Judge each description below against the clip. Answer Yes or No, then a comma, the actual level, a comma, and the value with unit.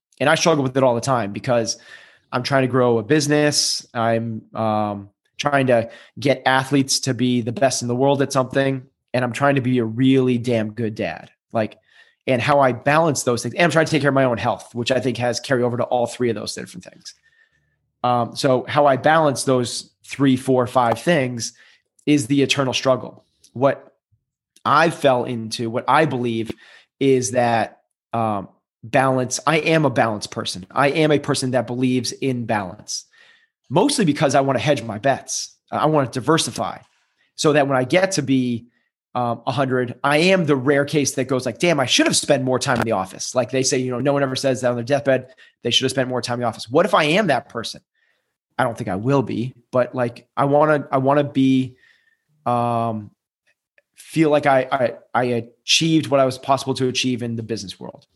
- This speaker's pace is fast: Yes, fast, 215 wpm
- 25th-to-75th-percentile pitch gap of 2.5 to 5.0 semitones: Yes, average, 2.9 semitones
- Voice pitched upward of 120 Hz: Yes, low, 130 Hz